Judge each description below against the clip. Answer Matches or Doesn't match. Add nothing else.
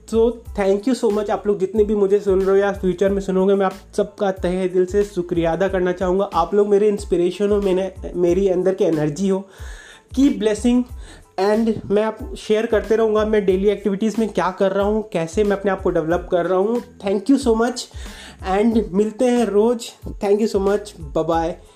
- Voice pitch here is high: Matches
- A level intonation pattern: Matches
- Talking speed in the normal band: Doesn't match